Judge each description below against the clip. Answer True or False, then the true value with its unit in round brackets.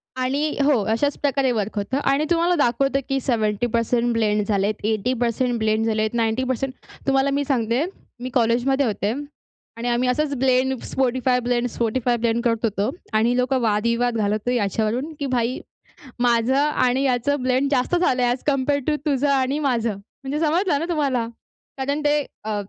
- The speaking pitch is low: False (250 Hz)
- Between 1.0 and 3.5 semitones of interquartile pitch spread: True (3.1 semitones)